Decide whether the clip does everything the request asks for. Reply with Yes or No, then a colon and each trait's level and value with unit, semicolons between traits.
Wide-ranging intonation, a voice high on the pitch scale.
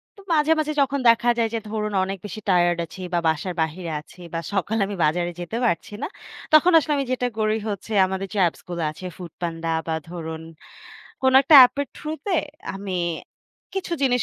Yes: wide, 6.7 semitones; high, 200 Hz